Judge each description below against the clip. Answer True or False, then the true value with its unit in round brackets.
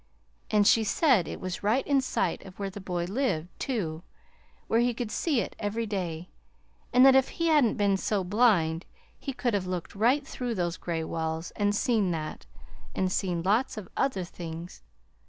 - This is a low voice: False (205 Hz)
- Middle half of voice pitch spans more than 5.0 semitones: True (5.4 semitones)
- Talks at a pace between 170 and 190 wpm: True (185 wpm)